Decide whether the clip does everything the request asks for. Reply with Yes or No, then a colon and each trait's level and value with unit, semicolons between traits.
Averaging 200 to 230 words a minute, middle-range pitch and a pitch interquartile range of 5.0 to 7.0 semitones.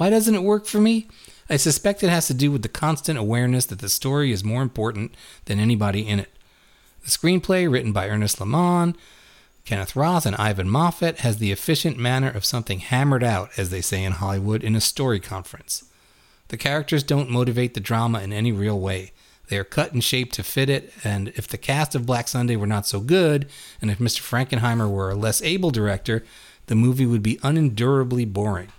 No: fast, 205 wpm; low, 120 Hz; wide, 5.4 semitones